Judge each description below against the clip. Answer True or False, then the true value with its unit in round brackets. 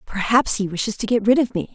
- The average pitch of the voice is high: True (220 Hz)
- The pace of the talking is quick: True (275 wpm)